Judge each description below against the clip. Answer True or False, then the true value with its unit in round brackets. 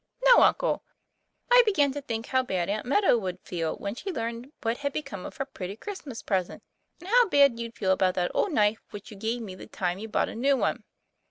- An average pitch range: False (6.3 semitones)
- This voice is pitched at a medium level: False (230 Hz)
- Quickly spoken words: True (235 wpm)